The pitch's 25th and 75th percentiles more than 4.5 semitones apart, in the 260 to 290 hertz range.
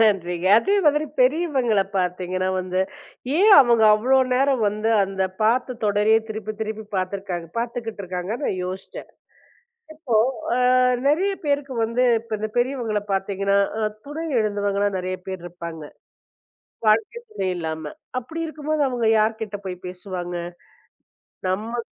No: average, 5.0 semitones; high, 215 Hz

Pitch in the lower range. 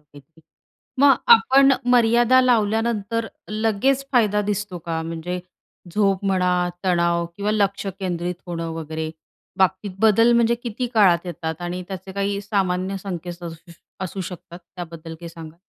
No: high, 190 Hz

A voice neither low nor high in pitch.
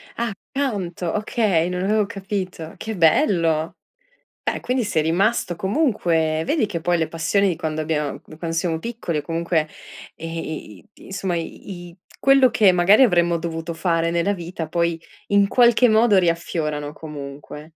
Yes: medium, 175 Hz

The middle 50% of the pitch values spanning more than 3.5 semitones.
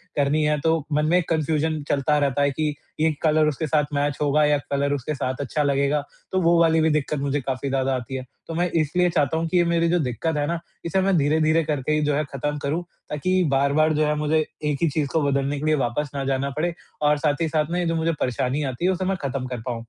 No: narrow, 2.5 semitones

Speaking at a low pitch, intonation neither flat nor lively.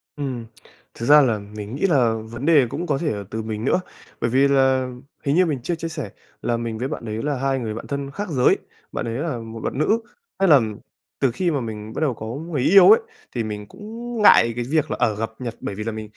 Yes: low, 130 Hz; average, 4.8 semitones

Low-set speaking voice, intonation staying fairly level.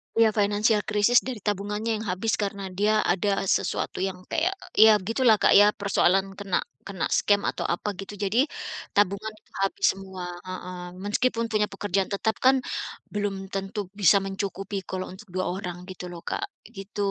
No: high, 205 Hz; narrow, 1.9 semitones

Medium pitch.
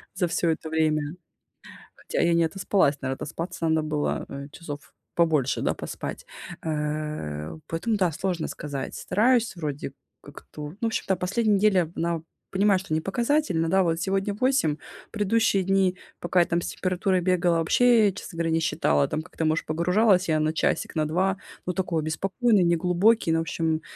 Yes: medium, 170 Hz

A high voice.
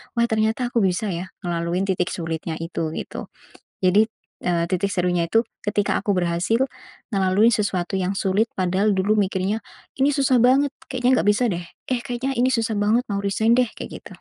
Yes: high, 200 Hz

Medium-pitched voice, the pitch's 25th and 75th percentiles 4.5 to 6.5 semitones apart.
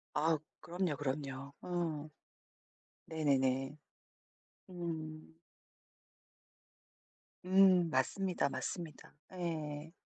No: medium, 155 Hz; average, 3.3 semitones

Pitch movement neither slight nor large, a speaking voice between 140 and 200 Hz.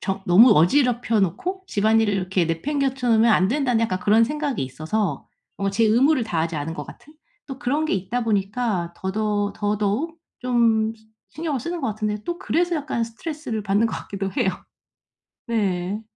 No: average, 4.8 semitones; high, 220 Hz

